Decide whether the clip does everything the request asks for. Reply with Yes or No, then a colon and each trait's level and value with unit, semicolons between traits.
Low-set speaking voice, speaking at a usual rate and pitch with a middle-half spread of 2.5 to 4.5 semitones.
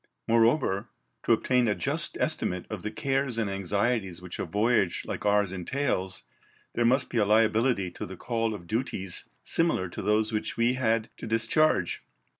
Yes: low, 110 Hz; average, 170 wpm; average, 3.8 semitones